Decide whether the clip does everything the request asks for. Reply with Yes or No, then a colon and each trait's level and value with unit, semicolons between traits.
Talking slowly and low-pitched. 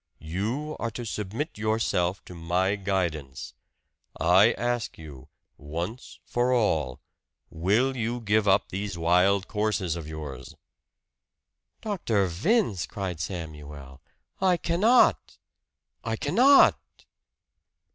Yes: slow, 105 wpm; low, 100 Hz